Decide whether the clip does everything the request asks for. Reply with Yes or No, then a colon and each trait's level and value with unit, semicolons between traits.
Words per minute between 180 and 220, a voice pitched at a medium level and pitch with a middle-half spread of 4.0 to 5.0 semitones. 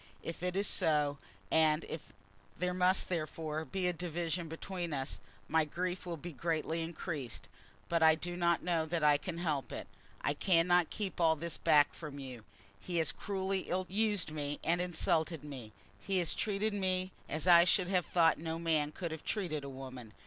No: average, 185 wpm; medium, 165 Hz; average, 2.7 semitones